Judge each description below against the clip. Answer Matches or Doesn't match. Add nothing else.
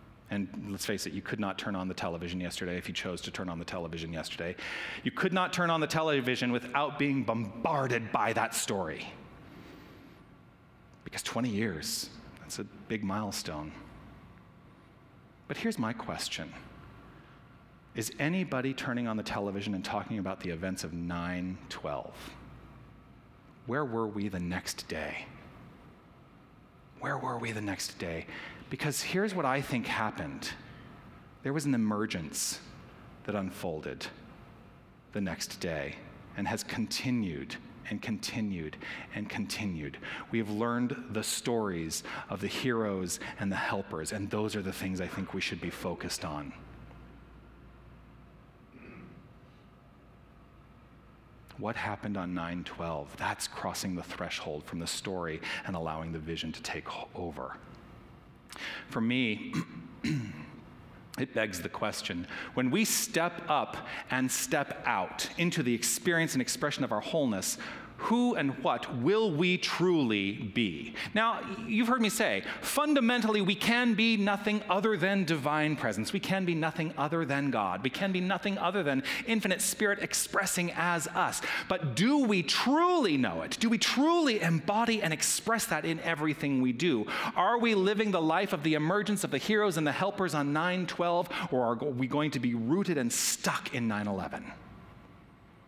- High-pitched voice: Doesn't match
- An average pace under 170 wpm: Matches